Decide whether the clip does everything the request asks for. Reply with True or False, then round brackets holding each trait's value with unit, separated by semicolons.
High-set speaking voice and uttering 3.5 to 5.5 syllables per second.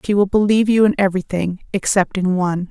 False (195 Hz; 6.6 syllables/s)